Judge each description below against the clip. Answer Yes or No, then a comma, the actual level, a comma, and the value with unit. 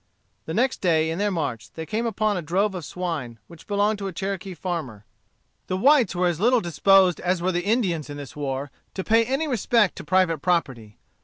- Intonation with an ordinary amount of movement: Yes, average, 4.4 semitones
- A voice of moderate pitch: Yes, medium, 180 Hz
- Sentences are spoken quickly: Yes, fast, 210 wpm